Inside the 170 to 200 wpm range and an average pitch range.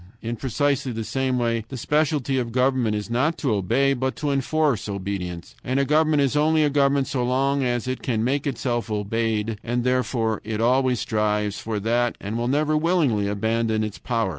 Yes: average, 190 wpm; average, 3.8 semitones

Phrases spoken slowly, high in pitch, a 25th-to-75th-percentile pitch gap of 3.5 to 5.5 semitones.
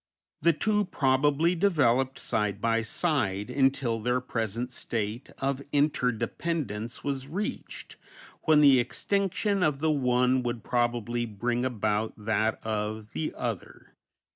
No: slow, 125 wpm; low, 125 Hz; average, 4.6 semitones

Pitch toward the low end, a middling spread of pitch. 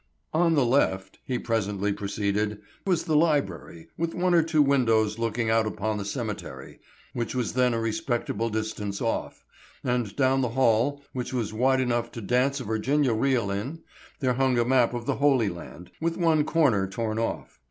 Yes: low, 120 Hz; average, 4.1 semitones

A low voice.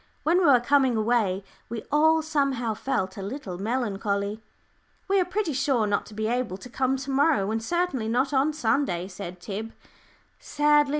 No: high, 245 Hz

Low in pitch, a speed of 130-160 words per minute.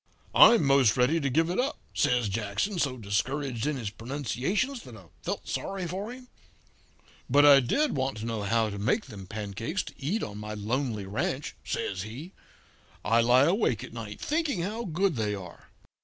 No: low, 130 Hz; average, 185 wpm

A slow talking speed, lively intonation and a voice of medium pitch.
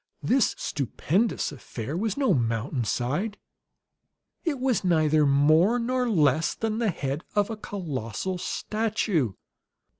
Yes: slow, 115 wpm; wide, 7.9 semitones; medium, 175 Hz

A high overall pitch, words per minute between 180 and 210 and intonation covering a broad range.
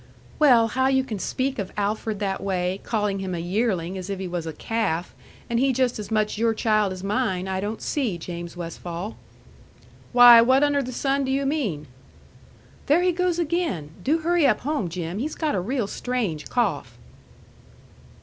Yes: high, 215 Hz; average, 185 wpm; wide, 6.1 semitones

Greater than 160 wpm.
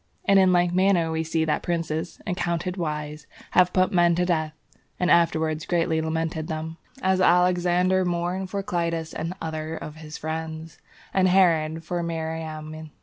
No: average, 155 wpm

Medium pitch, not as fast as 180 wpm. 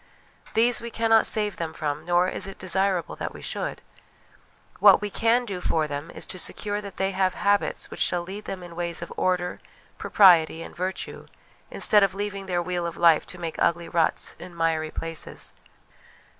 No: medium, 180 Hz; average, 185 wpm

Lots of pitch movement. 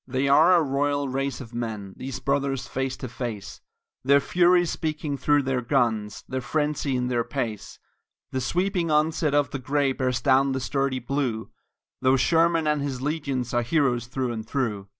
No: average, 2.8 semitones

